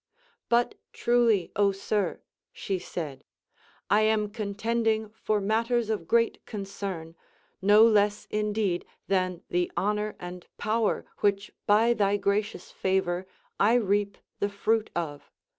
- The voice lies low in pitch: No, high, 205 Hz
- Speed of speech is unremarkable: No, slow, 125 wpm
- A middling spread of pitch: No, narrow, 2.3 semitones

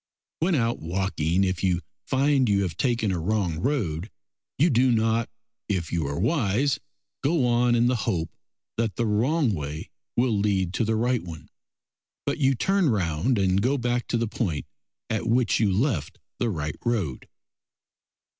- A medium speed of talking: Yes, average, 165 wpm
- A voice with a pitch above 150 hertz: No, low, 110 Hz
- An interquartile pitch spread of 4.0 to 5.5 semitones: Yes, average, 5.2 semitones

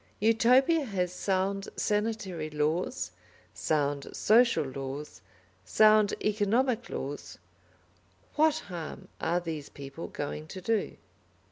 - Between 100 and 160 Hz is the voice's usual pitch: No, high, 190 Hz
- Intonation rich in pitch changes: Yes, wide, 6.5 semitones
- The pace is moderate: No, slow, 100 wpm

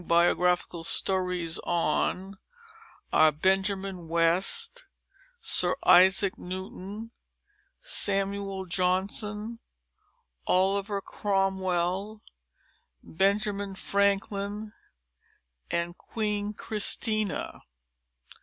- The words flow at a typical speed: No, slow, 50 wpm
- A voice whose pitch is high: Yes, high, 195 Hz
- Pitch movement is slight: Yes, narrow, 2.2 semitones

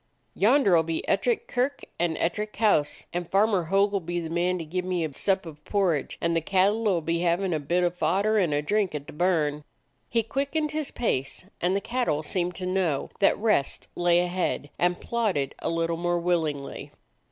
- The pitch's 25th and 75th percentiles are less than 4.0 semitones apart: Yes, average, 3.6 semitones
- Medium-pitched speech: Yes, medium, 180 Hz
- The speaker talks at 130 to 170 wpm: No, fast, 205 wpm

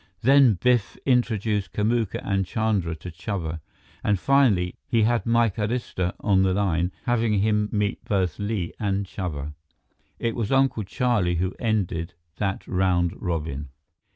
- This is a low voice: Yes, low, 100 Hz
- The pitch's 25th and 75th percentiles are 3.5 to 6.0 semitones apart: Yes, average, 4.1 semitones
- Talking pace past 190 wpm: No, average, 140 wpm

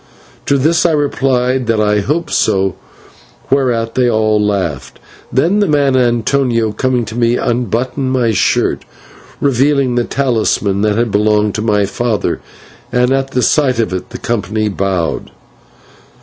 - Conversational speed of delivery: Yes, average, 150 wpm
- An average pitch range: Yes, average, 3.8 semitones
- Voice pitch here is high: No, low, 120 Hz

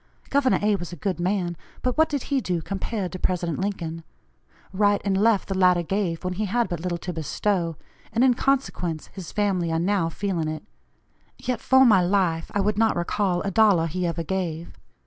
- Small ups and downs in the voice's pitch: No, average, 3.3 semitones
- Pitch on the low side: No, medium, 185 Hz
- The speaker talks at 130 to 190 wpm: No, average, 200 wpm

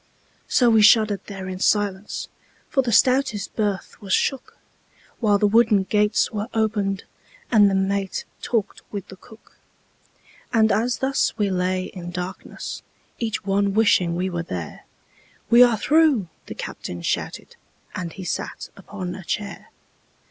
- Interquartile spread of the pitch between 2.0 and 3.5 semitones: Yes, average, 2.8 semitones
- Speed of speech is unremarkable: Yes, average, 150 wpm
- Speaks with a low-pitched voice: No, high, 205 Hz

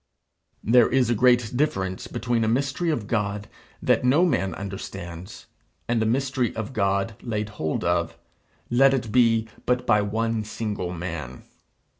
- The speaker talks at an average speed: Yes, average, 150 wpm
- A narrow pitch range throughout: No, average, 3.7 semitones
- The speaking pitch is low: Yes, low, 110 Hz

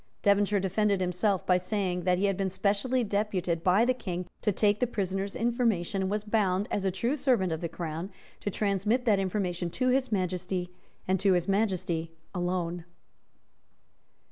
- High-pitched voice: Yes, high, 195 Hz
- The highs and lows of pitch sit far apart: No, average, 2.7 semitones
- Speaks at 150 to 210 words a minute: Yes, average, 170 wpm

